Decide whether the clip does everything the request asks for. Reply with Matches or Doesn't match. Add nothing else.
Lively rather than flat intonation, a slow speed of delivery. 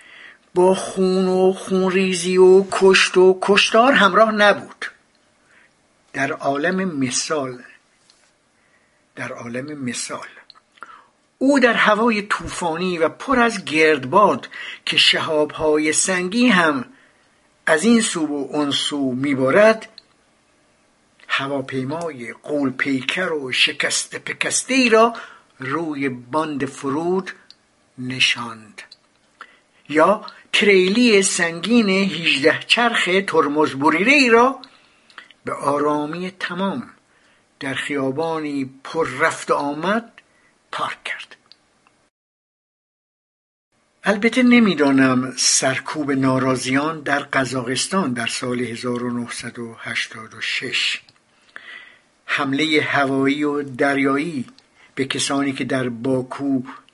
Matches